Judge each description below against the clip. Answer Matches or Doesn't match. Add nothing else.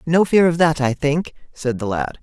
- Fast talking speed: Matches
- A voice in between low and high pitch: Matches